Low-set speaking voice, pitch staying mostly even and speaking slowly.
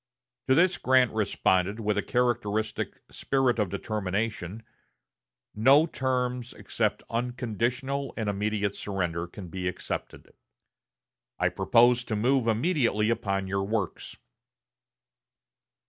No: low, 110 Hz; average, 3.6 semitones; slow, 105 wpm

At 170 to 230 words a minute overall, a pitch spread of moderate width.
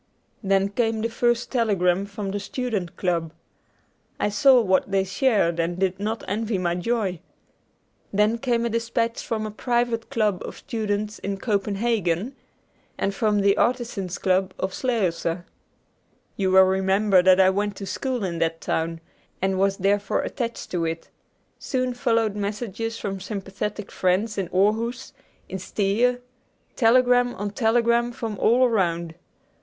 No: average, 145 wpm; average, 3.4 semitones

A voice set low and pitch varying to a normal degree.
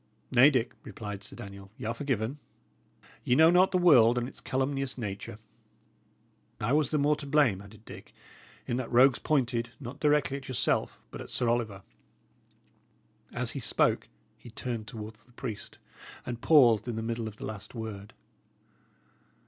Yes: low, 120 Hz; average, 3.8 semitones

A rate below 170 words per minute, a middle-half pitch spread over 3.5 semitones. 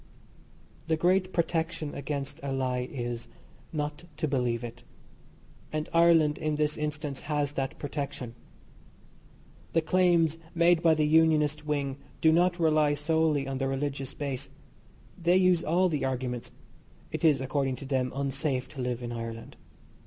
No: average, 145 wpm; average, 3.2 semitones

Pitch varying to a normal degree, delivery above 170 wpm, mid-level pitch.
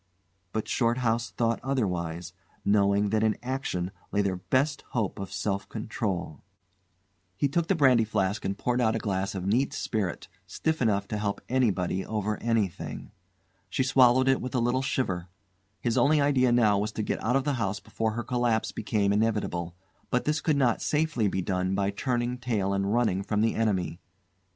No: average, 4.1 semitones; average, 180 wpm; low, 110 Hz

